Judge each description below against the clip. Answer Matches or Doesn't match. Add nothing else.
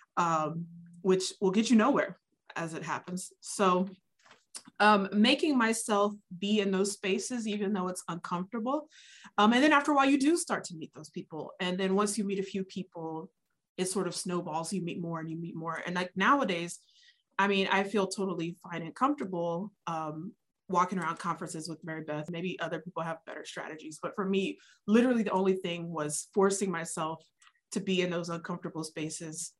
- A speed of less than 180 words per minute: Doesn't match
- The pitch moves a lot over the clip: Doesn't match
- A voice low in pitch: Doesn't match